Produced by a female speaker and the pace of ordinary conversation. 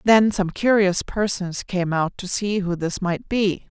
Yes: female; average, 190 wpm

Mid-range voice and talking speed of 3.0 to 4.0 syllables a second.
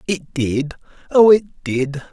Yes: medium, 160 Hz; 3.8 syllables/s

